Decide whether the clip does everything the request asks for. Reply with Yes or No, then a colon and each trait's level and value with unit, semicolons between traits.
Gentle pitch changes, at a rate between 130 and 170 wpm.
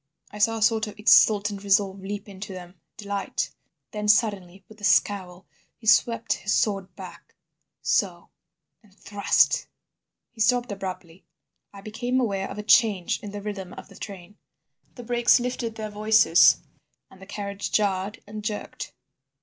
Yes: narrow, 2.0 semitones; average, 145 wpm